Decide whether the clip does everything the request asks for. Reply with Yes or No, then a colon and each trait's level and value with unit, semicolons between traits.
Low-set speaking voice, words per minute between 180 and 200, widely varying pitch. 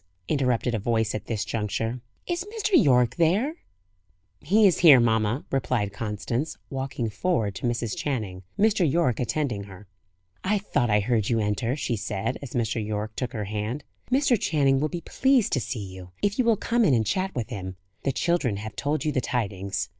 Yes: low, 125 Hz; average, 190 wpm; wide, 6.8 semitones